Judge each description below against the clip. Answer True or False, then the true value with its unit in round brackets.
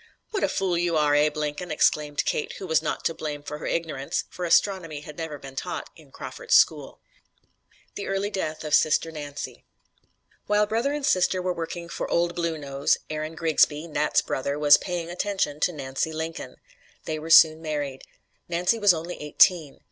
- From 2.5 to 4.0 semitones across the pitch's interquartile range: True (2.9 semitones)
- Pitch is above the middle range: False (160 Hz)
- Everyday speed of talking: True (180 wpm)